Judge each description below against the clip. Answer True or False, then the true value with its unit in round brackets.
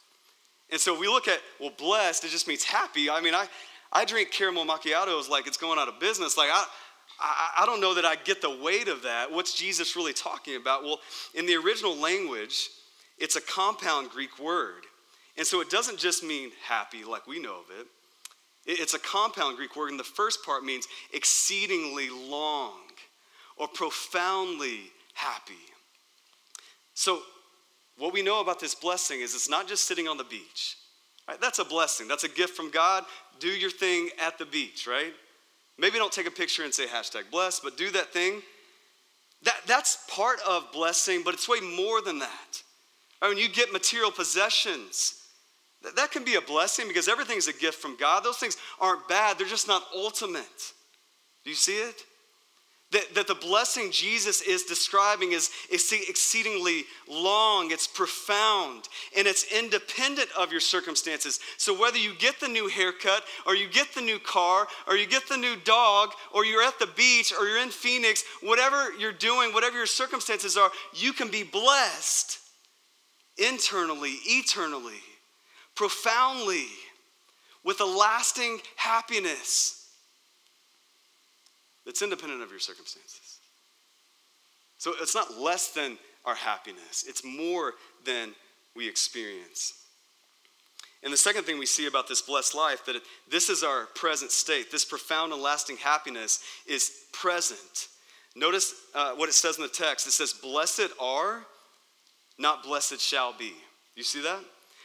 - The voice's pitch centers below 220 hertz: False (225 Hz)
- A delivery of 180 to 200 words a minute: False (165 wpm)